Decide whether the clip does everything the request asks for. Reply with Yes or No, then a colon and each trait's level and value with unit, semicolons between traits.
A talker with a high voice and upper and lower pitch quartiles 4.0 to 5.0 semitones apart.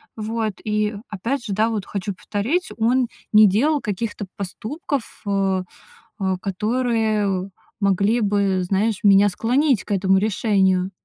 No: high, 210 Hz; average, 2.7 semitones